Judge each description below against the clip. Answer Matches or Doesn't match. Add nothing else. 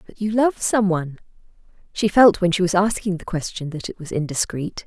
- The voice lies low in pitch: Doesn't match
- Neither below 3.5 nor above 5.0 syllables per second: Doesn't match